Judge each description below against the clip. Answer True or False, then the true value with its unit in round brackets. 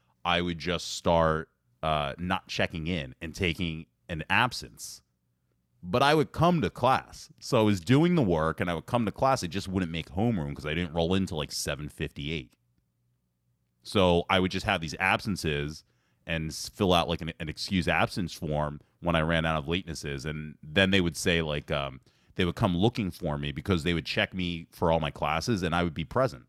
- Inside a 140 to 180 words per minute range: False (205 wpm)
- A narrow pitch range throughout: False (3.8 semitones)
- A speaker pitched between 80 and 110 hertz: True (85 Hz)